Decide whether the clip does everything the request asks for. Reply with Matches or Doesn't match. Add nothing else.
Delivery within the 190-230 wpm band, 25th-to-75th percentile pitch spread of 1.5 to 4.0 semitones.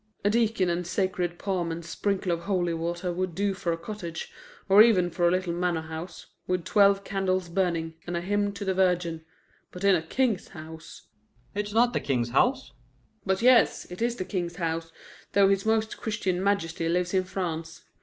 Matches